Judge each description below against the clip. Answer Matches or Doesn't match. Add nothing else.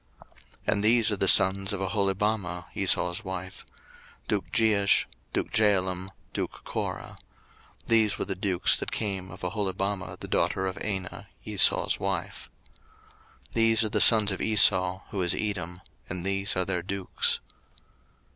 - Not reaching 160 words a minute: Matches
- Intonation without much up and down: Matches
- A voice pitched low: Matches